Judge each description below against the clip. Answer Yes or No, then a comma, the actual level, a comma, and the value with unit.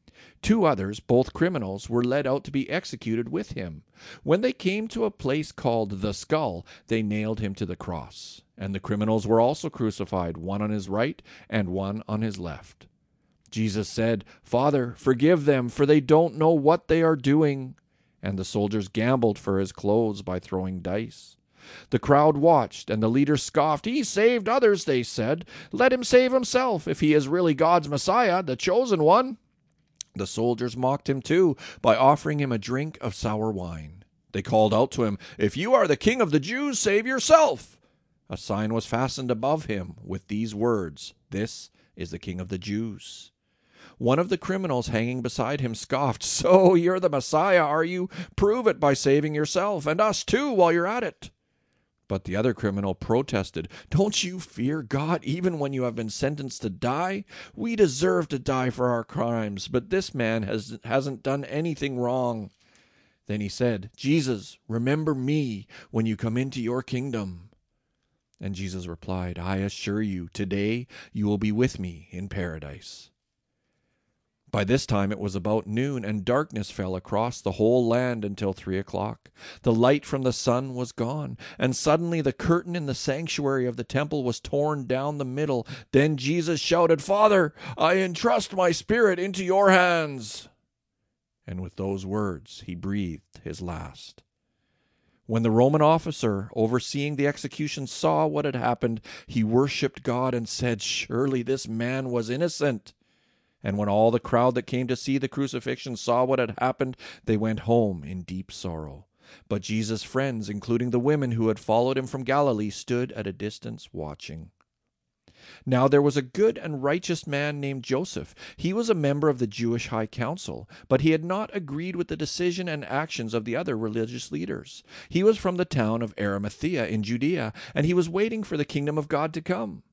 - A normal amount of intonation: No, wide, 6.1 semitones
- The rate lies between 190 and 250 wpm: No, average, 180 wpm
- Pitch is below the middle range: Yes, low, 125 Hz